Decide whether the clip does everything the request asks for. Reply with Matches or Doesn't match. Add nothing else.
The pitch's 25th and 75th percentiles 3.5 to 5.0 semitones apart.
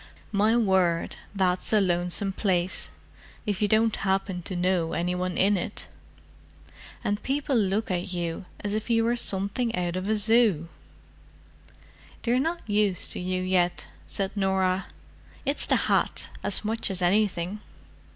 Doesn't match